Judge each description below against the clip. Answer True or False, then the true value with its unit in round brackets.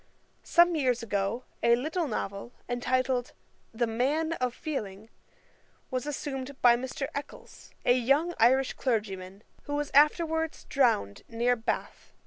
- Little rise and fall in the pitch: False (3.9 semitones)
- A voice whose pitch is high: True (255 Hz)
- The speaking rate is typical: False (125 wpm)